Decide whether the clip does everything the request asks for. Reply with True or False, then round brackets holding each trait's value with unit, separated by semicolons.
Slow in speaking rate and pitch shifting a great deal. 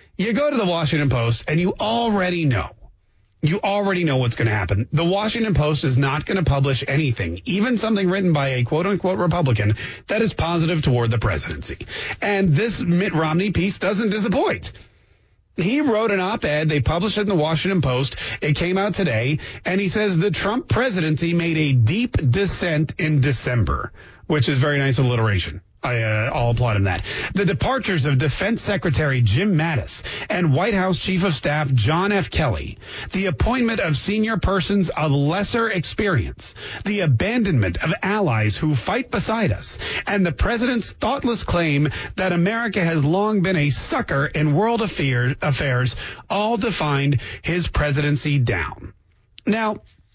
False (170 wpm; 8.1 semitones)